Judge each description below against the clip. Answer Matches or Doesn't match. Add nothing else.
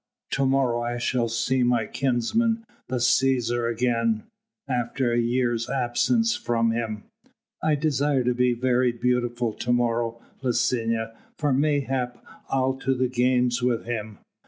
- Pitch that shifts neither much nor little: Doesn't match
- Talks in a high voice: Doesn't match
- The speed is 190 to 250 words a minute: Doesn't match